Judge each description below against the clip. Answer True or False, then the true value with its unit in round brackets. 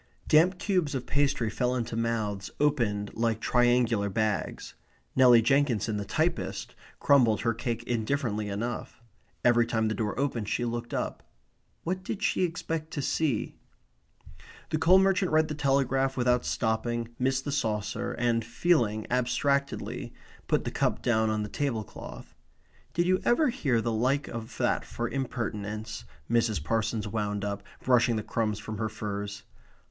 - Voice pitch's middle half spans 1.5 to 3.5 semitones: False (4.2 semitones)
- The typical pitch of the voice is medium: False (120 Hz)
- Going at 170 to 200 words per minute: False (150 wpm)